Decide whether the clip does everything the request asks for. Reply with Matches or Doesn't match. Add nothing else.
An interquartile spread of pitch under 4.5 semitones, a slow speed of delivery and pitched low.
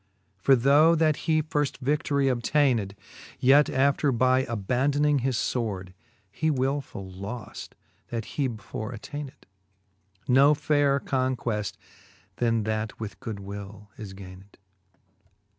Doesn't match